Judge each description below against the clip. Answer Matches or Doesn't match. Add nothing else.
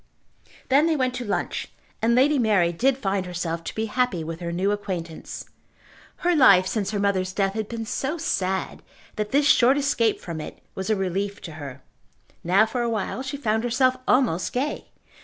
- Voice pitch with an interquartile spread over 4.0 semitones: Matches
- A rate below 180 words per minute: Doesn't match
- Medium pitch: Doesn't match